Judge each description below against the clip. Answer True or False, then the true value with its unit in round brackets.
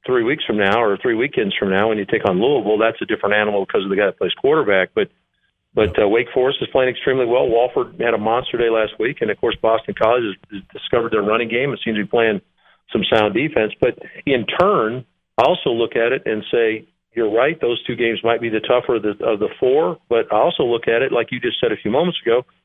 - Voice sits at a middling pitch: False (115 Hz)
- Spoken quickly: True (255 wpm)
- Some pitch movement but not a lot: True (3.2 semitones)